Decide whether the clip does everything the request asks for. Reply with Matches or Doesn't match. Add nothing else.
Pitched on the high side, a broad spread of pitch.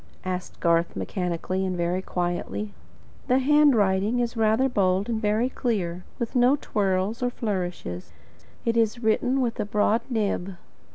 Doesn't match